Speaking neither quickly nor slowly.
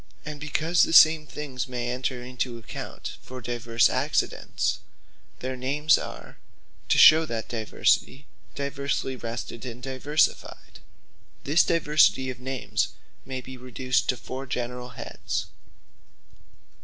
No: slow, 120 wpm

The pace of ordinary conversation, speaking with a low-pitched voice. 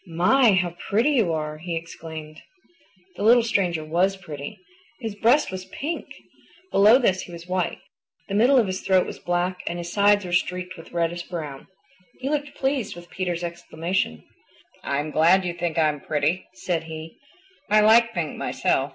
No: average, 170 wpm; medium, 180 Hz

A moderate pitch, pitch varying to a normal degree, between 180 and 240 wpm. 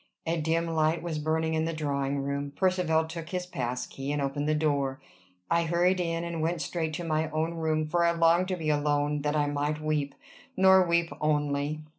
No: medium, 155 Hz; narrow, 2.3 semitones; fast, 205 wpm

